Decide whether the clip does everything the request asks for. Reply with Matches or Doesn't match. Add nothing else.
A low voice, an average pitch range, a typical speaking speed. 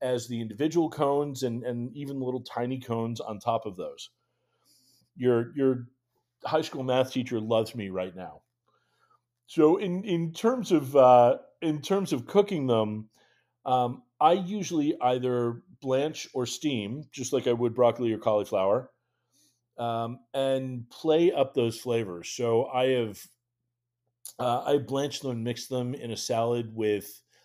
Matches